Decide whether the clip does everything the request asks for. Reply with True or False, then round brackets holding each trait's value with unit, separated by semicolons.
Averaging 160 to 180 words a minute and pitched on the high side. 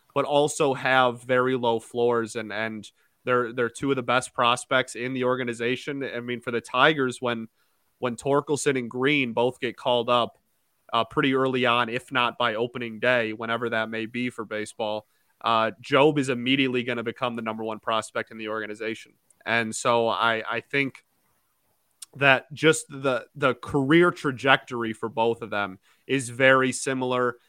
False (170 wpm; 120 Hz)